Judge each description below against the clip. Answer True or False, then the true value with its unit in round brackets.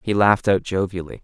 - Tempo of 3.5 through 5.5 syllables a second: False (6.2 syllables/s)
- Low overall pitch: True (95 Hz)